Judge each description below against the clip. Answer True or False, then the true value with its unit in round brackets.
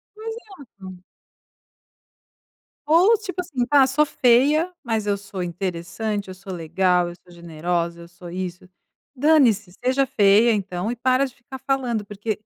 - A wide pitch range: True (6.9 semitones)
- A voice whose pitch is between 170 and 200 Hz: False (215 Hz)